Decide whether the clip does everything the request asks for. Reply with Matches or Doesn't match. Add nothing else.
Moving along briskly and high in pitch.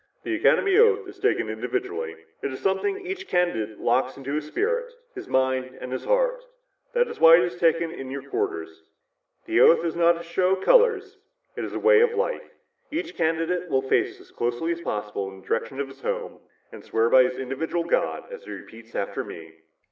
Doesn't match